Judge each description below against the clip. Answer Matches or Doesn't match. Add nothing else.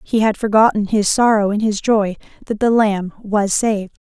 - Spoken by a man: Doesn't match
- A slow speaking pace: Doesn't match